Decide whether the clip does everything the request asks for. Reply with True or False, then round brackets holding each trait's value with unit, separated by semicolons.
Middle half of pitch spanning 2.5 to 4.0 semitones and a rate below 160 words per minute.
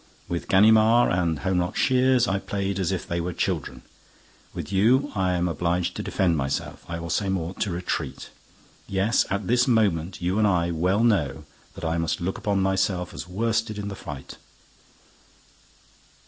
False (3.5 semitones; 170 wpm)